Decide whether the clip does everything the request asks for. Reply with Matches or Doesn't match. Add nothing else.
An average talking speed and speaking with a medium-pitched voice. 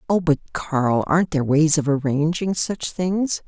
Matches